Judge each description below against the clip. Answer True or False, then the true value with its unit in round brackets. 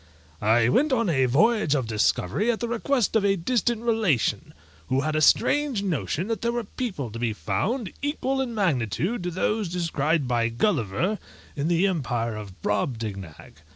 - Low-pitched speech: False (170 Hz)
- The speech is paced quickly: False (170 wpm)